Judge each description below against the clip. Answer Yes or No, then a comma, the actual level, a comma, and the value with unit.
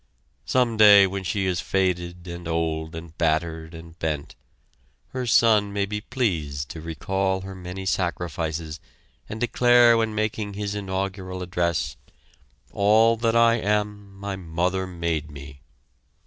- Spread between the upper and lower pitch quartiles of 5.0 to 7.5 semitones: No, average, 3.9 semitones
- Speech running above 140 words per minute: No, slow, 135 wpm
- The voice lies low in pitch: Yes, very low, 95 Hz